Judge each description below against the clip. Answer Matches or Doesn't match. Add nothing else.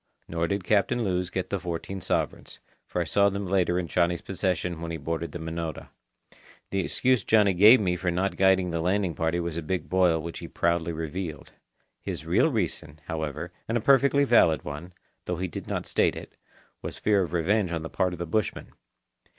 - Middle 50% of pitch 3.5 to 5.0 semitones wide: Doesn't match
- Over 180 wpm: Matches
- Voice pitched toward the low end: Matches